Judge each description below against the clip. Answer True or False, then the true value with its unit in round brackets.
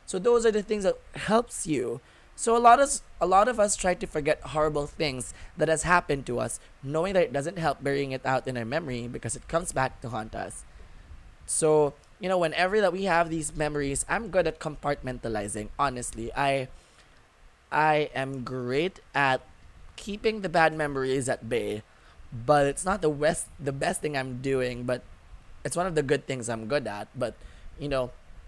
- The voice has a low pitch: False (145 Hz)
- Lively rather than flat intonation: False (4.9 semitones)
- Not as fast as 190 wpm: False (195 wpm)